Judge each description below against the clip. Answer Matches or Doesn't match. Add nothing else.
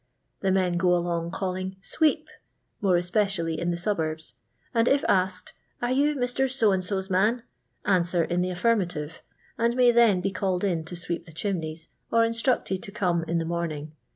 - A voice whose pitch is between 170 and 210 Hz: Matches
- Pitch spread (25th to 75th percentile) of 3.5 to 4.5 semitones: Matches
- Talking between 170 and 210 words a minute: Matches